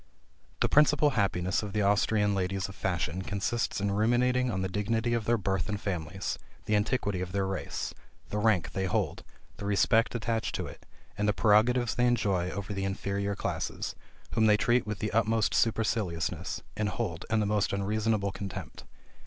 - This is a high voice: No, low, 105 Hz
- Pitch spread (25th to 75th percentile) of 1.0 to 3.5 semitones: Yes, narrow, 2.6 semitones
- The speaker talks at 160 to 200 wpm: Yes, average, 180 wpm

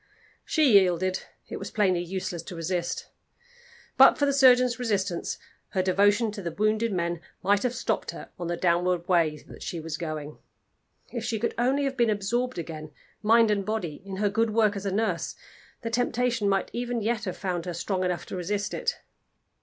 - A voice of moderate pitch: No, high, 200 Hz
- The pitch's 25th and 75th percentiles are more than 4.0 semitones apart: Yes, average, 4.6 semitones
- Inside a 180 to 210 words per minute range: Yes, average, 190 wpm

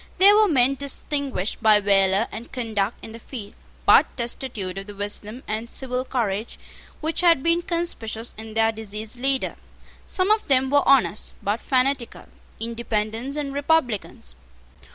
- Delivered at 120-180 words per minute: Yes, average, 150 wpm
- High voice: Yes, high, 240 Hz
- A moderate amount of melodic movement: Yes, average, 4.4 semitones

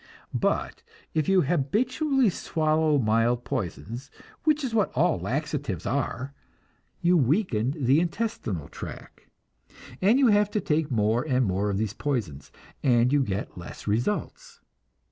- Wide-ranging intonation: Yes, wide, 7.7 semitones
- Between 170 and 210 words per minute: No, slow, 135 wpm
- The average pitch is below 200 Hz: Yes, medium, 140 Hz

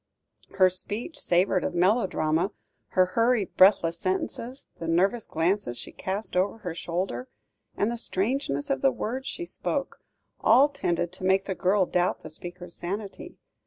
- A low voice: No, medium, 185 Hz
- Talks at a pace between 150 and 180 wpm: Yes, average, 155 wpm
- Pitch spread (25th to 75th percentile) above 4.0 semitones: No, average, 3.7 semitones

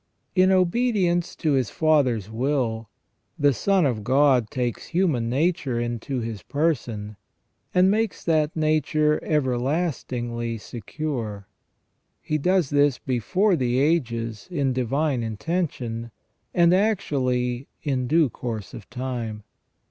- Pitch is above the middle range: No, low, 135 Hz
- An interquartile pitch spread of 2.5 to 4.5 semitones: No, wide, 5.4 semitones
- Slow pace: Yes, slow, 115 wpm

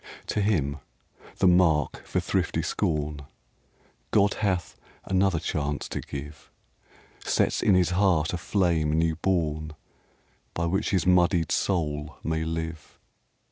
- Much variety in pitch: No, average, 3.3 semitones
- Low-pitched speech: Yes, very low, 85 Hz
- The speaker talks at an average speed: No, slow, 125 wpm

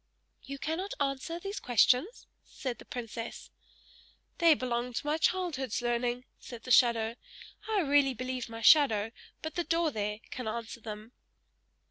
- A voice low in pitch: No, very high, 255 Hz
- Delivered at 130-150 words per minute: Yes, average, 145 wpm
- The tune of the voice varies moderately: Yes, average, 5.0 semitones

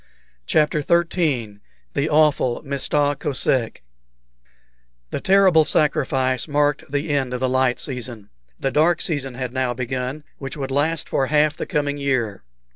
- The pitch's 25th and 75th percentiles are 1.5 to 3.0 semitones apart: Yes, average, 2.7 semitones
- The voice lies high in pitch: No, medium, 140 Hz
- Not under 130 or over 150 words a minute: Yes, average, 140 wpm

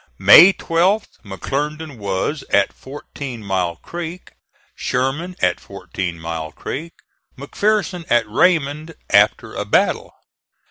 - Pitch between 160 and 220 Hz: No, medium, 140 Hz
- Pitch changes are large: Yes, wide, 8.6 semitones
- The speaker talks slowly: Yes, slow, 105 wpm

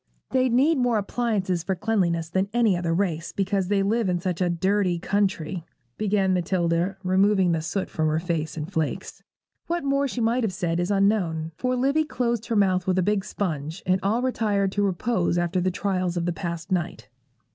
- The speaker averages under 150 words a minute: No, average, 195 wpm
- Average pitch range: Yes, average, 3.6 semitones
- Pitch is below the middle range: No, high, 190 Hz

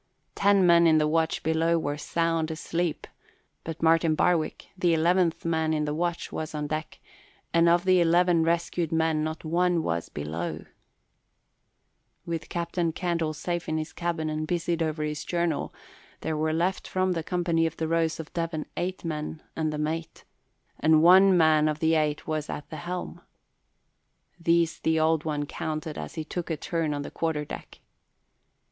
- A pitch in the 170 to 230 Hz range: No, medium, 160 Hz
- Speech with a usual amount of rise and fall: No, narrow, 1.6 semitones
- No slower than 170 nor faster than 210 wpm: Yes, average, 175 wpm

